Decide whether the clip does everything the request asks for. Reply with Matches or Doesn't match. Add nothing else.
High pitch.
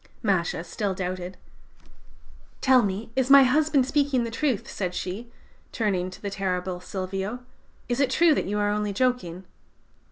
Matches